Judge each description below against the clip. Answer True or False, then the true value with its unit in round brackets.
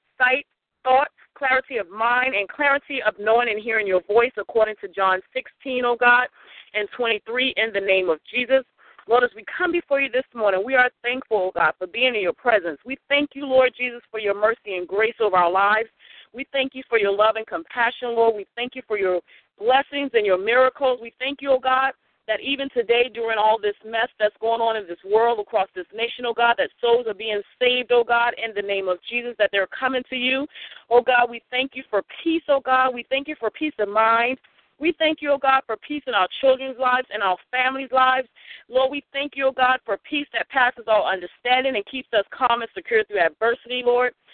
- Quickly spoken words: True (235 wpm)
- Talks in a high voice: True (240 Hz)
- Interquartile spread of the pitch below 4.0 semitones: True (3.3 semitones)